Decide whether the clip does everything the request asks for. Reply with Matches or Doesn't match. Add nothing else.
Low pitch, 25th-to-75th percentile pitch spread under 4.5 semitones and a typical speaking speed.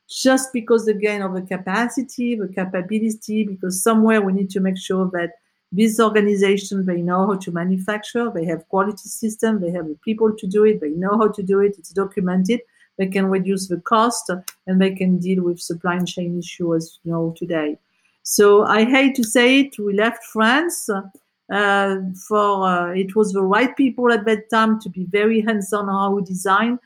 Doesn't match